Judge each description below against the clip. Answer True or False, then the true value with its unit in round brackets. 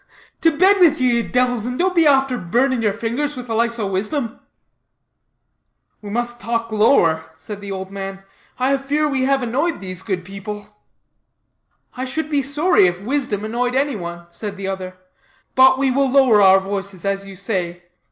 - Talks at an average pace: True (180 wpm)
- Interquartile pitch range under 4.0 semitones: False (5.5 semitones)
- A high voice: True (230 Hz)